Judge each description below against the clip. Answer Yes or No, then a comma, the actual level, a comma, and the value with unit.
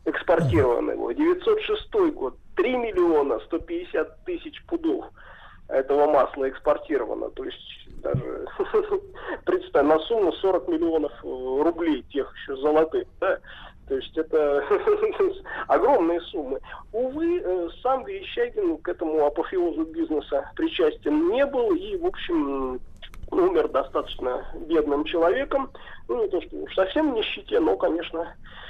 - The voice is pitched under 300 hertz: No, very high, 340 Hz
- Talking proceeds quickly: No, average, 115 wpm